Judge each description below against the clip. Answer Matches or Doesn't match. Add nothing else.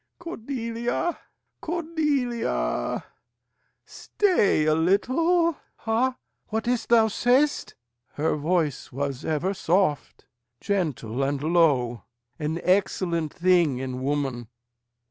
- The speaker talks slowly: Matches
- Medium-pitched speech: Matches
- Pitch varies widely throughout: Matches